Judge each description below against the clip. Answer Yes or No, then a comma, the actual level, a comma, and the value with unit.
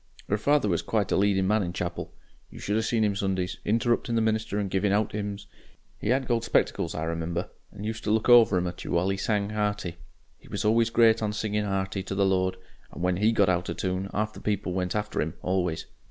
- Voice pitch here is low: Yes, low, 100 Hz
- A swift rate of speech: Yes, fast, 240 wpm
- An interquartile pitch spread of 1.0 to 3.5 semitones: Yes, narrow, 2.6 semitones